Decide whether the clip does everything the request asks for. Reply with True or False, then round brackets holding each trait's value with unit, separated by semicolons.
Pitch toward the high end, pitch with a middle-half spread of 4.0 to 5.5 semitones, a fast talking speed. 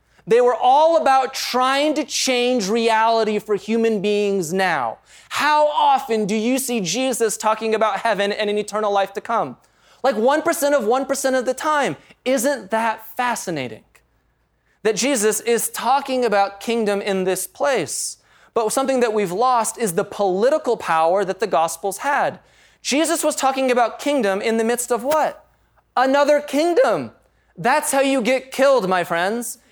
False (235 Hz; 4.4 semitones; 155 wpm)